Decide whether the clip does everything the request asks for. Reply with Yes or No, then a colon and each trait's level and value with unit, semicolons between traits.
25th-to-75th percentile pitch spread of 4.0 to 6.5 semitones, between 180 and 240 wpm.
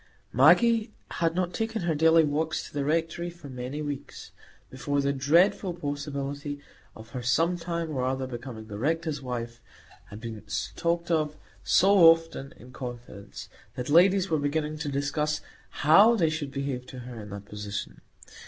No: average, 4.5 semitones; average, 160 wpm